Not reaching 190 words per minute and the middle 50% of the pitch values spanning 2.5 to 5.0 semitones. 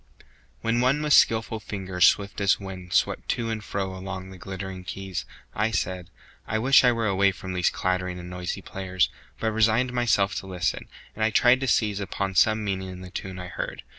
No: average, 200 wpm; average, 3.1 semitones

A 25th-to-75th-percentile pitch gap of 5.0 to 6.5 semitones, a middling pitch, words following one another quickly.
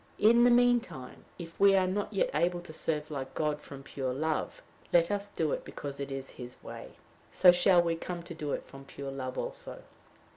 Yes: average, 5.3 semitones; medium, 165 Hz; fast, 215 wpm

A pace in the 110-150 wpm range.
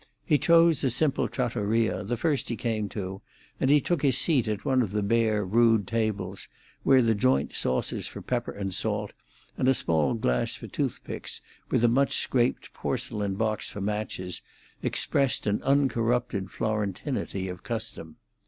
No: average, 160 wpm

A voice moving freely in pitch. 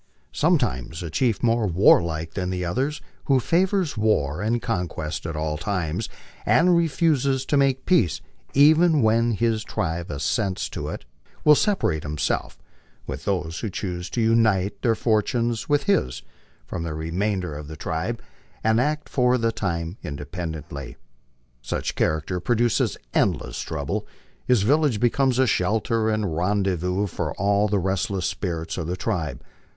Yes: wide, 6.2 semitones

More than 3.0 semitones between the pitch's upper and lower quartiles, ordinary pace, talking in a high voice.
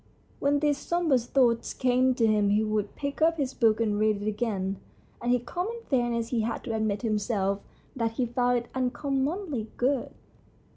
Yes: average, 3.7 semitones; average, 190 wpm; high, 240 Hz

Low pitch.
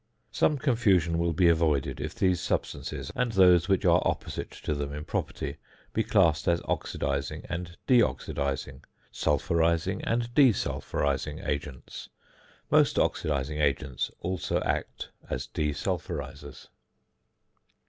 Yes: very low, 80 Hz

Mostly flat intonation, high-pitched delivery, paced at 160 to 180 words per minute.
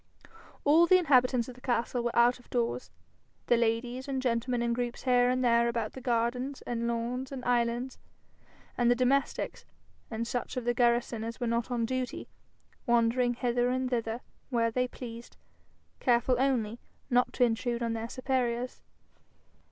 Yes: narrow, 1.3 semitones; high, 245 Hz; average, 165 wpm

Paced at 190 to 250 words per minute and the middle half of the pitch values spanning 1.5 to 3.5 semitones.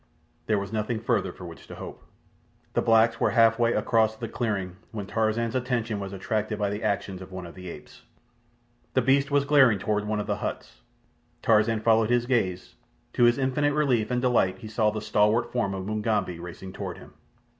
Yes: average, 200 wpm; average, 2.9 semitones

